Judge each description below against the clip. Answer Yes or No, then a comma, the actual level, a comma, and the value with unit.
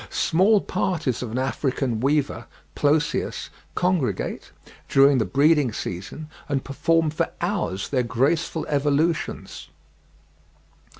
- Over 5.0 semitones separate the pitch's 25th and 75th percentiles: No, average, 4.2 semitones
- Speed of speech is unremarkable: No, slow, 105 wpm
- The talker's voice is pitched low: No, medium, 145 Hz